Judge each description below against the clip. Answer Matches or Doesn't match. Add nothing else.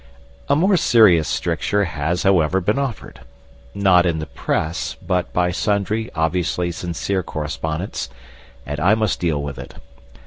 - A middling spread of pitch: Matches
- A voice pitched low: Matches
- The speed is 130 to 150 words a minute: Matches